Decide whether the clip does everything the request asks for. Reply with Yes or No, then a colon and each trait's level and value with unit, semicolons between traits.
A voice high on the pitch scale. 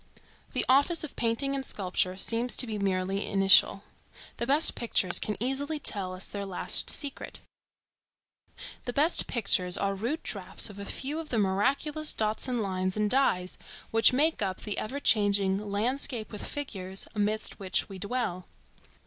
Yes: high, 215 Hz